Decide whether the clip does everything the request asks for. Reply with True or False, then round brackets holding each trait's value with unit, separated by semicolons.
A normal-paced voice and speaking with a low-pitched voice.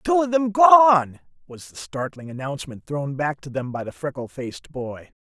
False (195 wpm; 150 Hz)